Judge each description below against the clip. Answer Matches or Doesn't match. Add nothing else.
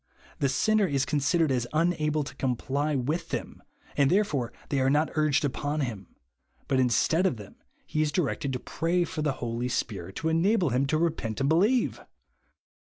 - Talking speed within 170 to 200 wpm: Matches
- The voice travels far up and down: Doesn't match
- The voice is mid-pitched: Matches